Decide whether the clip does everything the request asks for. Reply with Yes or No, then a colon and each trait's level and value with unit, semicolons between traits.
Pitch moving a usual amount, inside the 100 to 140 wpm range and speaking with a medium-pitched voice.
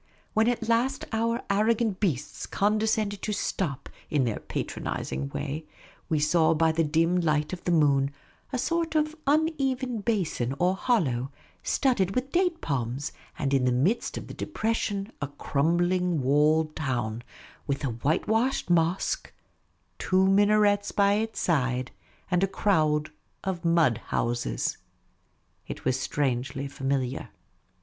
No: wide, 7.4 semitones; slow, 135 wpm; medium, 170 Hz